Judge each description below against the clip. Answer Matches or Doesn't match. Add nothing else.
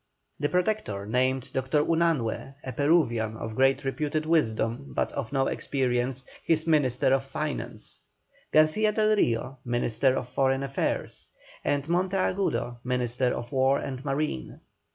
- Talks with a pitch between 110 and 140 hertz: Matches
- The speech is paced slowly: Matches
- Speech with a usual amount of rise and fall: Matches